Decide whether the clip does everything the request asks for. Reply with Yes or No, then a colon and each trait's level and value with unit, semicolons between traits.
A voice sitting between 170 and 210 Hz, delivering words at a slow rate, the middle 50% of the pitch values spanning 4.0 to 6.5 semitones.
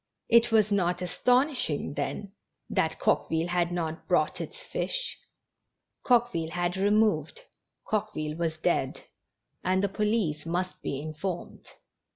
Yes: medium, 185 Hz; slow, 125 wpm; average, 4.6 semitones